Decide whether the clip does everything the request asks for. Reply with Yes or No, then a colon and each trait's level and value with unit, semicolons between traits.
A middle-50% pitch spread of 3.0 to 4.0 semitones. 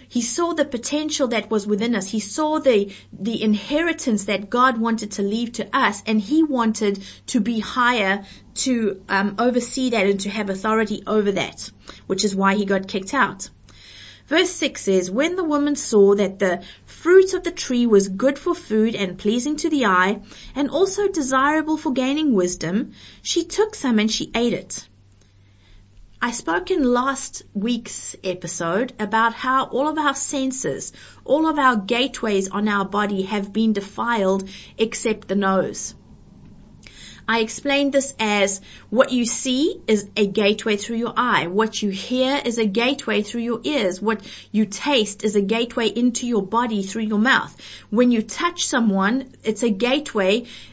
No: average, 4.6 semitones